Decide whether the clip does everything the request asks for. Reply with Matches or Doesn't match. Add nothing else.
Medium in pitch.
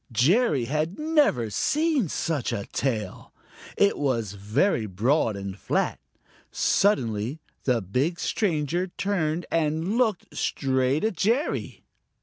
Matches